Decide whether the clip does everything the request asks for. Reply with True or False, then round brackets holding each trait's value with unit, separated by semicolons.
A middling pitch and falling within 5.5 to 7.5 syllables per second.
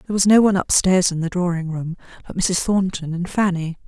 True (180 Hz; 6.0 syllables/s)